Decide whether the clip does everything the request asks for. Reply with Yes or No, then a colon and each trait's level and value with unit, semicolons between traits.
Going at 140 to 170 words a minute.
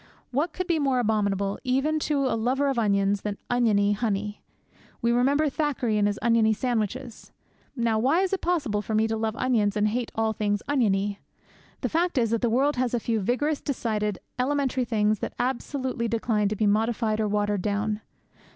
No: average, 190 wpm